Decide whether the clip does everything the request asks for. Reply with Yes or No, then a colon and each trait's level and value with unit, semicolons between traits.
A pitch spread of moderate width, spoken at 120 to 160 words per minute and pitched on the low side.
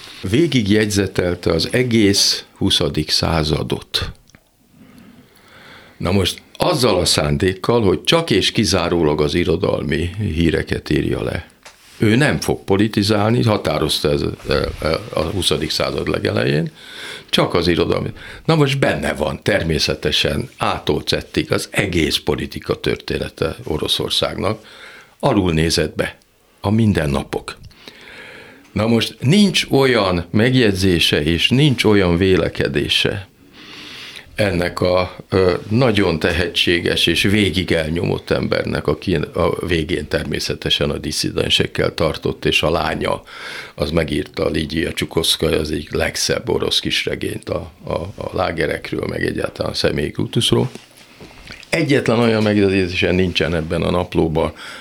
No: average, 5.0 semitones; average, 110 wpm; very low, 95 Hz